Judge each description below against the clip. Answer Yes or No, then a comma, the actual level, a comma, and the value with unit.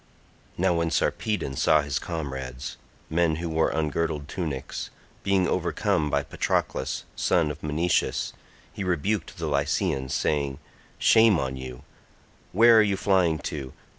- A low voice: Yes, very low, 80 Hz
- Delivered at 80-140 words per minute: Yes, slow, 135 wpm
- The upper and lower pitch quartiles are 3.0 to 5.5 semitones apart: Yes, average, 4.0 semitones